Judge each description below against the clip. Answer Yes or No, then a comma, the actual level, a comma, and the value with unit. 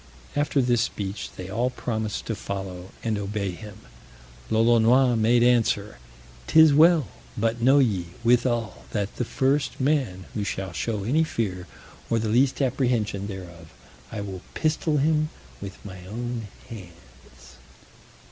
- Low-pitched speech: Yes, low, 115 Hz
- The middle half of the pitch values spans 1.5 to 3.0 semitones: No, average, 4.3 semitones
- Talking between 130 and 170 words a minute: Yes, average, 140 wpm